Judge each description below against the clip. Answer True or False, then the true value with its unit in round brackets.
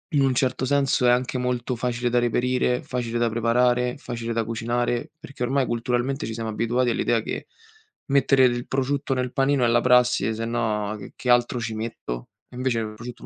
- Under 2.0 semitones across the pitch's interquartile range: True (1.5 semitones)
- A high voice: False (120 Hz)